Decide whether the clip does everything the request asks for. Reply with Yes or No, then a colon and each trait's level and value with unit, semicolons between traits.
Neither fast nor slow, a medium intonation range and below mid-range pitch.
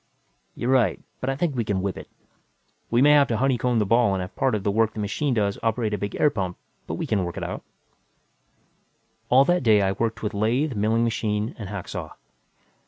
No: fast, 225 wpm; average, 3.6 semitones; low, 110 Hz